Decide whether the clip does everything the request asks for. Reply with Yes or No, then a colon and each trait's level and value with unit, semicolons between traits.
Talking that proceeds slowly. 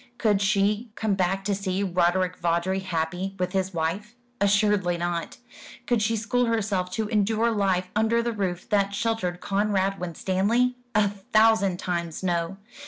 No: average, 150 wpm